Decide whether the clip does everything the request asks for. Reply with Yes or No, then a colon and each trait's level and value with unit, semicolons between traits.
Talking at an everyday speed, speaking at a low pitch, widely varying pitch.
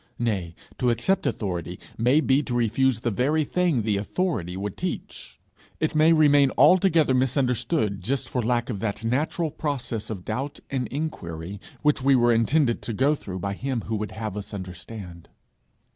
Yes: average, 170 wpm; low, 120 Hz; wide, 5.7 semitones